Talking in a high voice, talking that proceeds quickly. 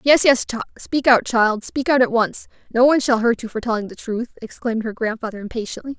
Yes: high, 235 Hz; fast, 220 wpm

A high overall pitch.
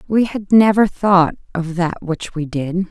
No: medium, 180 Hz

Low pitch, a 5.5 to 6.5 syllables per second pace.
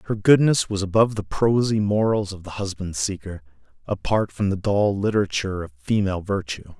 Yes: low, 100 Hz; 5.6 syllables/s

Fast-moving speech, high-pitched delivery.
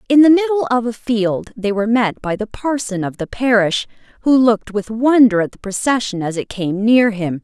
Yes: fast, 220 wpm; high, 225 Hz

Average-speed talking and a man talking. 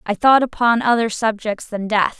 No: average, 190 wpm; female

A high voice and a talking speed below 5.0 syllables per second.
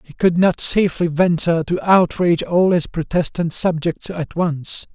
No: medium, 170 Hz; 4.6 syllables/s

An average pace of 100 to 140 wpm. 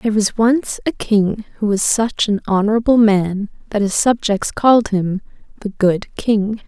No: average, 170 wpm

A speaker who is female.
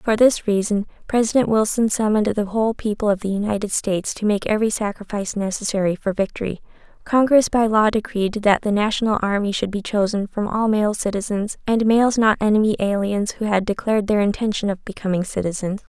Yes: female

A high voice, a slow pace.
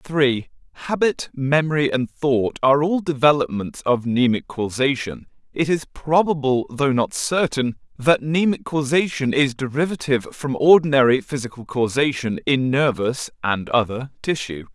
No: low, 135 Hz; slow, 125 wpm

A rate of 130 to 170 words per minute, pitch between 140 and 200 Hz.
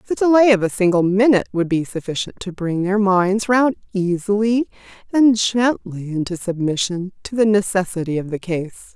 Yes: average, 165 wpm; high, 195 Hz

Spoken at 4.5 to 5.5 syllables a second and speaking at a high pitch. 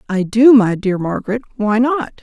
Yes: 5.0 syllables/s; high, 225 Hz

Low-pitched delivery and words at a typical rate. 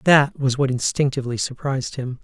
Yes: low, 130 Hz; average, 160 wpm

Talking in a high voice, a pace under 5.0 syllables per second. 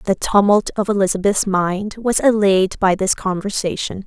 Yes: high, 200 Hz; 4.5 syllables/s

